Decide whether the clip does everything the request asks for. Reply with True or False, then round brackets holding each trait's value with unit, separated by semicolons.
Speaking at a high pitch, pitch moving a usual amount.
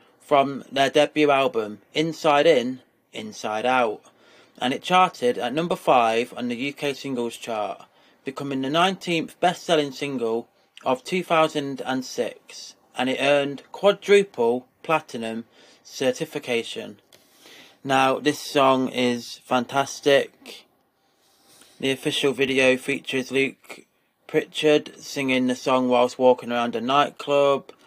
False (140 Hz; 3.5 semitones)